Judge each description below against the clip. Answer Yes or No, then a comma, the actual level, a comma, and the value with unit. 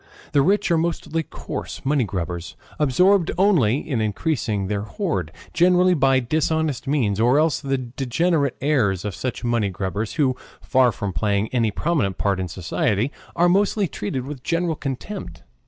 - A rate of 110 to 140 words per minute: No, average, 155 wpm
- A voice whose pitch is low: Yes, low, 130 Hz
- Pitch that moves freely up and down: Yes, wide, 7.5 semitones